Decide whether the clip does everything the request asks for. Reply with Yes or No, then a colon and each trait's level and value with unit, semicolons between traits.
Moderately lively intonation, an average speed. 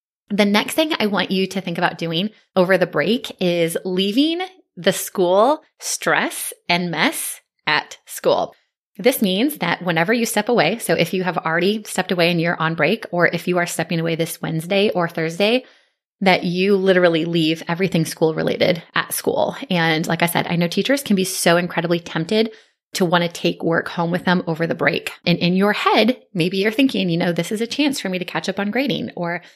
No: average, 3.7 semitones; fast, 210 wpm